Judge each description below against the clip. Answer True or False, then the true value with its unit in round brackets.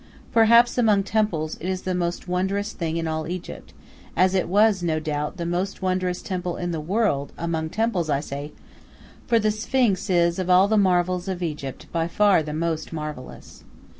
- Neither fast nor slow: True (185 wpm)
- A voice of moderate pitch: True (180 Hz)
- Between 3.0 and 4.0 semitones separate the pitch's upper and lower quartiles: True (3.5 semitones)